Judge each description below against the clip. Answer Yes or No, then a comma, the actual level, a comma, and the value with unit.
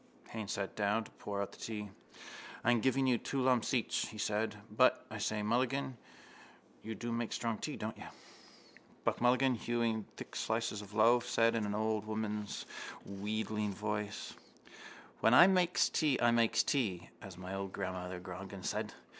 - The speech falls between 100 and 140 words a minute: No, average, 170 wpm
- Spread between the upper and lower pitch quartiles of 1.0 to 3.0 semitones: Yes, narrow, 2.4 semitones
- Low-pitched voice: Yes, low, 110 Hz